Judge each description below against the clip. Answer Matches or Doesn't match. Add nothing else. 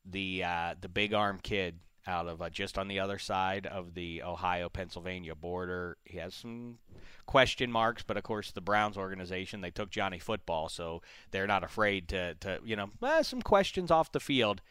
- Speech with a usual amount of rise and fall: Matches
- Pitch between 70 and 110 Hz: Matches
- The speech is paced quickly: Doesn't match